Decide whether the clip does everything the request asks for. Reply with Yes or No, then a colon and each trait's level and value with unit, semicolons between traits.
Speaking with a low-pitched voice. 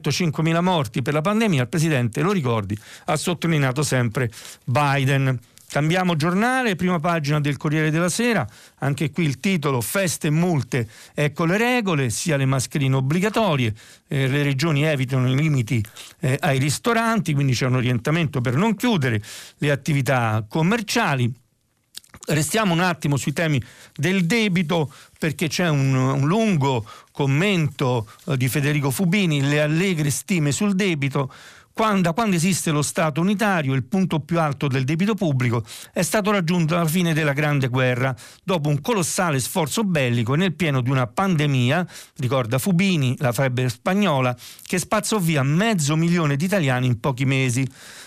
No: medium, 150 Hz